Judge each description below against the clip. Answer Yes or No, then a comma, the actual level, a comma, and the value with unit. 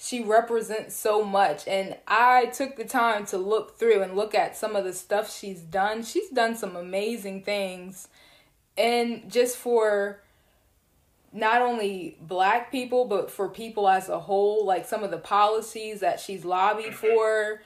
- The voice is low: No, high, 215 Hz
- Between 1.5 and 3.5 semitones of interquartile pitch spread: Yes, narrow, 2.6 semitones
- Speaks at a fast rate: No, average, 165 wpm